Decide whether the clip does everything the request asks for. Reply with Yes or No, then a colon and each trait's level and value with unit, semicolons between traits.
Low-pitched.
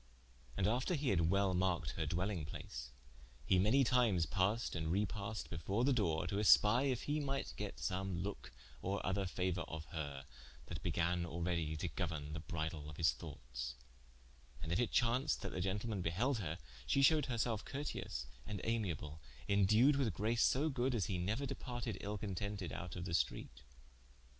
Yes: very low, 95 Hz